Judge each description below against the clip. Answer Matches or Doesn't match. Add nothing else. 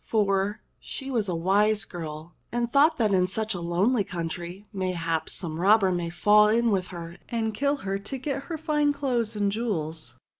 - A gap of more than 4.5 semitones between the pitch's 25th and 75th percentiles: Matches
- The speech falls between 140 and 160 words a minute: Doesn't match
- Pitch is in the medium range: Doesn't match